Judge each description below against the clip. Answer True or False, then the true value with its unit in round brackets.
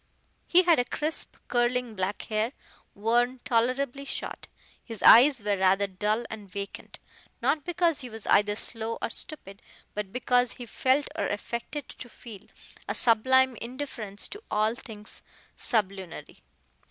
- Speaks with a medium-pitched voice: False (235 Hz)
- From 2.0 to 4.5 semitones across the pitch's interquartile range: True (3.8 semitones)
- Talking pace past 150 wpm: False (140 wpm)